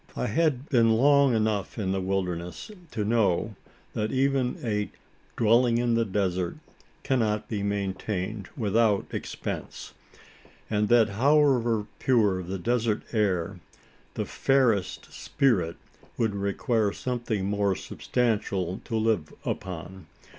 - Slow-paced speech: Yes, slow, 120 wpm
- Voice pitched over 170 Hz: No, low, 110 Hz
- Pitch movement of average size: Yes, average, 3.5 semitones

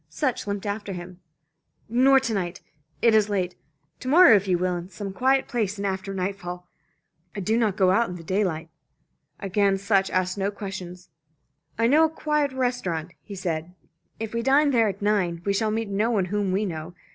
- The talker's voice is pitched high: Yes, high, 200 Hz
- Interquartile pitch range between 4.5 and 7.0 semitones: No, average, 3.7 semitones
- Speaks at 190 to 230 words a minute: Yes, average, 200 wpm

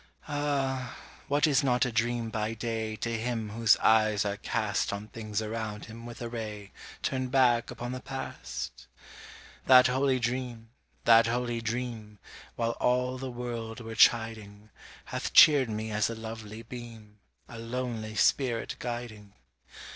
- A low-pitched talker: Yes, low, 115 Hz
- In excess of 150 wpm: No, average, 145 wpm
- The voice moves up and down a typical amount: No, narrow, 2.2 semitones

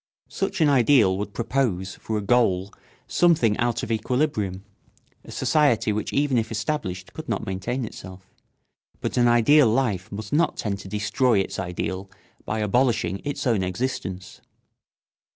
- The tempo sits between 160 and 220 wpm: No, average, 150 wpm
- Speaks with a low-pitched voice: Yes, low, 110 Hz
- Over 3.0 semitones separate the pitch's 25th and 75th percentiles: Yes, average, 4.9 semitones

